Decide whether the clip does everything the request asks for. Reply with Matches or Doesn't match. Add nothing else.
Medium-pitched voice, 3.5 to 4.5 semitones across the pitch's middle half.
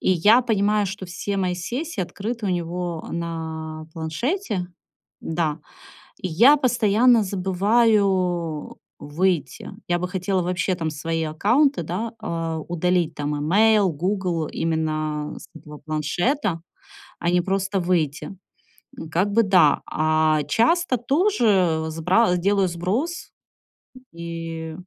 Matches